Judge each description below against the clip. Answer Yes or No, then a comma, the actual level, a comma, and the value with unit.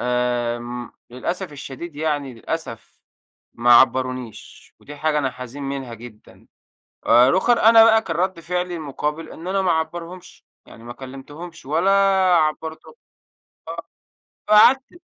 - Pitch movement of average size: No, wide, 5.8 semitones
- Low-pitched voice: No, medium, 150 Hz